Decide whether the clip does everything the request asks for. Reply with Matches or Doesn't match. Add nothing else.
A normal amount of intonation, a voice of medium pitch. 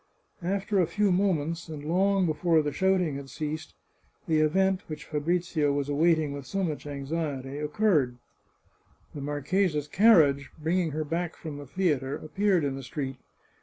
Matches